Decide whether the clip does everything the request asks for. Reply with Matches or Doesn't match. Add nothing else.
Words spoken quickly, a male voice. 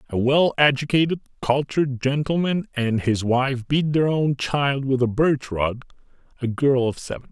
Doesn't match